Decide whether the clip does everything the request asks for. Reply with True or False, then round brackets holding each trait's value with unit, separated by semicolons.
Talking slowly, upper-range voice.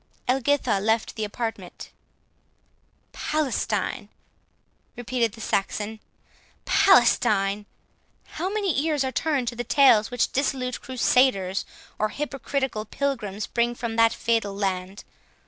True (110 wpm; 235 Hz)